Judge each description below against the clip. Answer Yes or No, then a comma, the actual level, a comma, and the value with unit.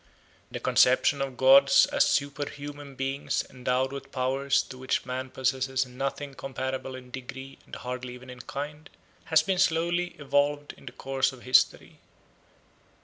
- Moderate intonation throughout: No, narrow, 1.7 semitones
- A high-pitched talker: No, low, 135 Hz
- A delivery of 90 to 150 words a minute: Yes, average, 145 wpm